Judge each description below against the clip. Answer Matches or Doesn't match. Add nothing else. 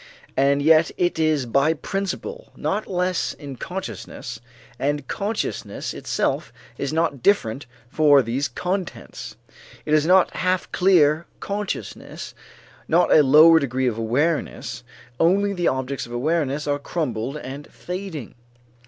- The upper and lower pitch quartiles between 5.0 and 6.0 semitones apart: Doesn't match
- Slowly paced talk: Matches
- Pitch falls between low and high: Matches